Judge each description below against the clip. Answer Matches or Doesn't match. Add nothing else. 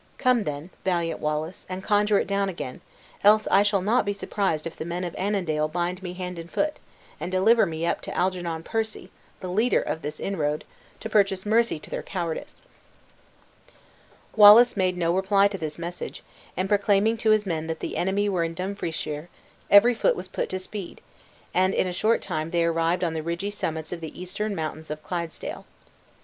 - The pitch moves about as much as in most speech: Matches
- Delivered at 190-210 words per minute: Matches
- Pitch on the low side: Doesn't match